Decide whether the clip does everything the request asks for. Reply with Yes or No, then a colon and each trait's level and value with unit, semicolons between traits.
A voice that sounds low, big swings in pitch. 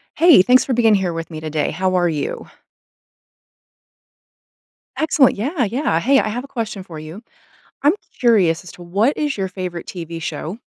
No: high, 190 Hz; wide, 6.7 semitones